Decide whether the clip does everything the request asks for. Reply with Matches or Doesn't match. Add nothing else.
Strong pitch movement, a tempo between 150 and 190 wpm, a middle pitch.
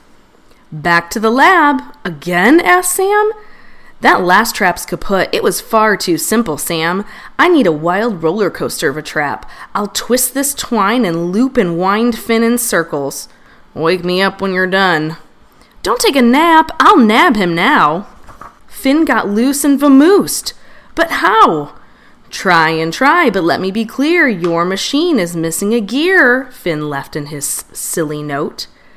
Doesn't match